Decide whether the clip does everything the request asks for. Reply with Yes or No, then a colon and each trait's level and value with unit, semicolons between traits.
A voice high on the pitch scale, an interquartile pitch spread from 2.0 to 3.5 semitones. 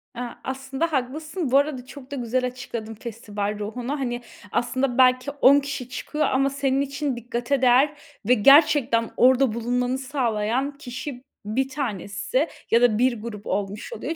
Yes: very high, 255 Hz; average, 2.8 semitones